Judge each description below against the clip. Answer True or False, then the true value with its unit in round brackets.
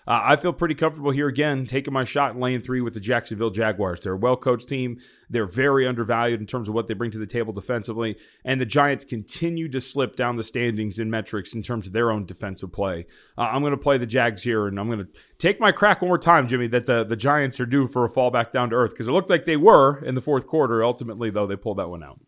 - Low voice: True (125 Hz)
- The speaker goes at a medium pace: False (275 wpm)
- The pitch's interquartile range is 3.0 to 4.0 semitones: True (3.6 semitones)